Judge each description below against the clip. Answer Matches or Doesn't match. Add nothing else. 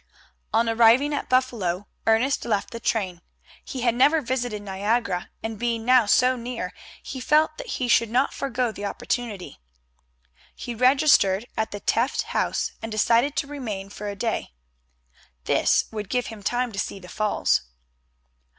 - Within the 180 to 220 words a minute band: Doesn't match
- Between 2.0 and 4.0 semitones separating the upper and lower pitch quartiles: Matches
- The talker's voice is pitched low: Doesn't match